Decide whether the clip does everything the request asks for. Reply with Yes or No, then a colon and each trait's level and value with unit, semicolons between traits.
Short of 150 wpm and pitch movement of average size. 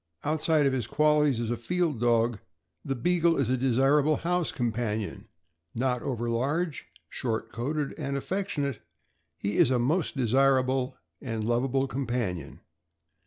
Yes: average, 140 wpm; average, 4.0 semitones